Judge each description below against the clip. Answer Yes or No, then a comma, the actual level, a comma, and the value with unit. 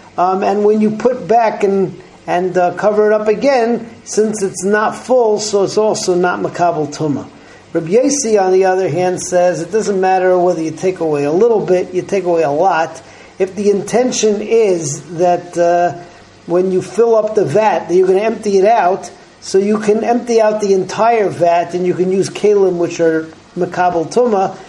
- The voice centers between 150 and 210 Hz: Yes, high, 190 Hz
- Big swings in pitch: No, average, 3.1 semitones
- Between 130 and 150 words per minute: No, average, 195 wpm